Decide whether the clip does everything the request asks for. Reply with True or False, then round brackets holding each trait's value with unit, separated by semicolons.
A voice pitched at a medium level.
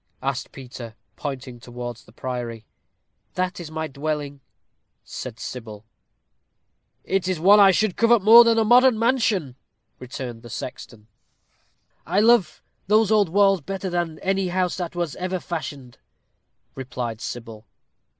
True (160 Hz)